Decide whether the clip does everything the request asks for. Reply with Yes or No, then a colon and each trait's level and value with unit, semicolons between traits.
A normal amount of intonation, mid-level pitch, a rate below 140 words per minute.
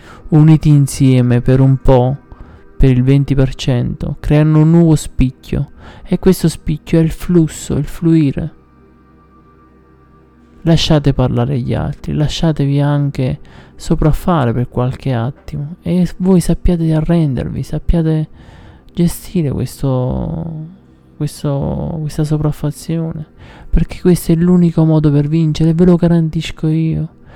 Yes: average, 3.8 semitones; medium, 150 Hz; slow, 115 wpm